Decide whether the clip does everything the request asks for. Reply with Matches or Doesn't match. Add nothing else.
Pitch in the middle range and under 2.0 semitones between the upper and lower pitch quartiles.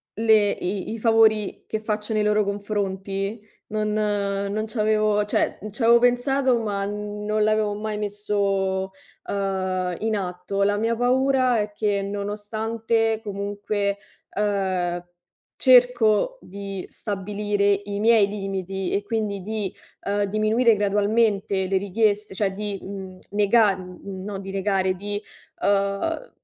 Doesn't match